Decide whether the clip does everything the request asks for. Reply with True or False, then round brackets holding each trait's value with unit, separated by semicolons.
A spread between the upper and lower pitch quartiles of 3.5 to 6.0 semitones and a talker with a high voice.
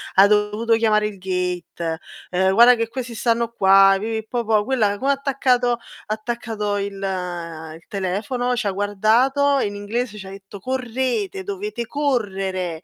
True (4.1 semitones; 215 Hz)